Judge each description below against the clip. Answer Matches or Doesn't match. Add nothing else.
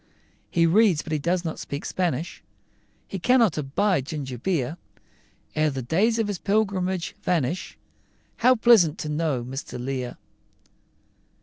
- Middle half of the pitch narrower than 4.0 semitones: Doesn't match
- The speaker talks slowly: Matches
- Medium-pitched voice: Matches